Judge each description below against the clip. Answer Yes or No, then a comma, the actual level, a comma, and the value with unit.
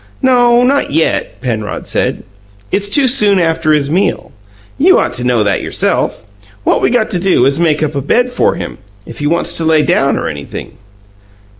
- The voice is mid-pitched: Yes, medium, 165 Hz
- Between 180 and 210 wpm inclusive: Yes, average, 195 wpm